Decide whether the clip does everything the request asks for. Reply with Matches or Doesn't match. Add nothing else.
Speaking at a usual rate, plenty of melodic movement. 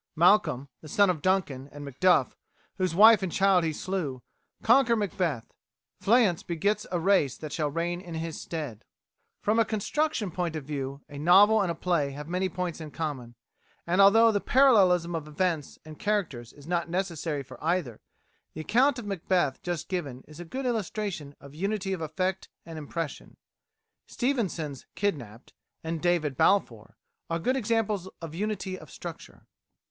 Doesn't match